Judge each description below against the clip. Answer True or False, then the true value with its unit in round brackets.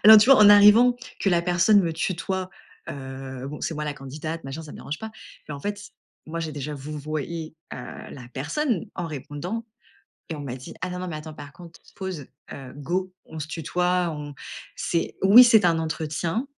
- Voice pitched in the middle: True (165 Hz)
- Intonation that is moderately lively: True (4.2 semitones)